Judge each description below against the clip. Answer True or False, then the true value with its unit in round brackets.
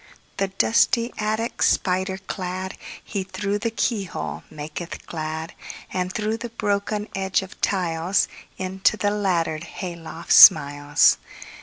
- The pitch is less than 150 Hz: False (190 Hz)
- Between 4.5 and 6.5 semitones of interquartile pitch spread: False (3.7 semitones)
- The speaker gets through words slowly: True (110 wpm)